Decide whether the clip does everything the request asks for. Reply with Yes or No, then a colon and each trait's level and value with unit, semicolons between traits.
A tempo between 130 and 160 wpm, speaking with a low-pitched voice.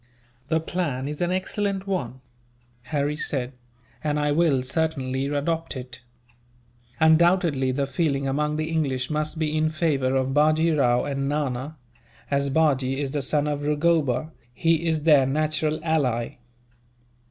No: average, 140 wpm; medium, 150 Hz